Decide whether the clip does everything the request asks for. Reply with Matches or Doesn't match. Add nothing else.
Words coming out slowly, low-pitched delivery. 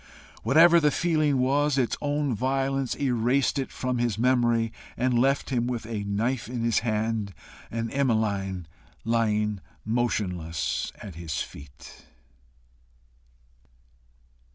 Matches